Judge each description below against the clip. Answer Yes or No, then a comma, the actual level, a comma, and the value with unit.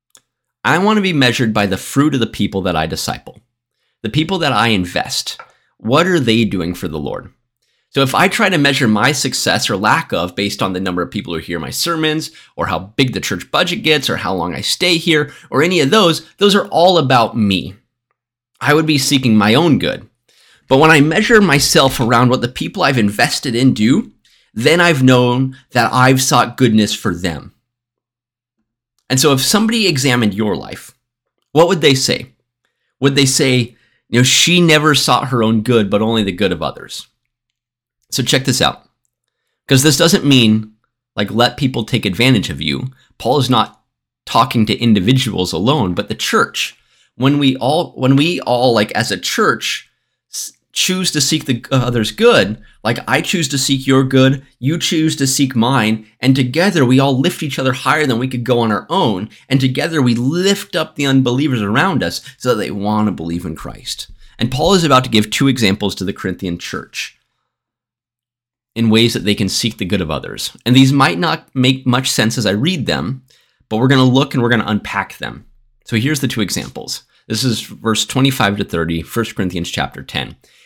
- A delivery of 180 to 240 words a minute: Yes, average, 200 wpm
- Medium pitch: No, low, 125 Hz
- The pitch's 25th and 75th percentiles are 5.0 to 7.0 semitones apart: No, average, 4.0 semitones